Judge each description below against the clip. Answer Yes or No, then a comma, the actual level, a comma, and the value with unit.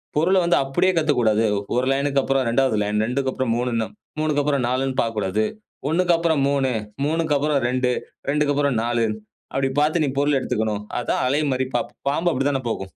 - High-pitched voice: No, low, 135 Hz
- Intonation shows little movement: No, average, 3.3 semitones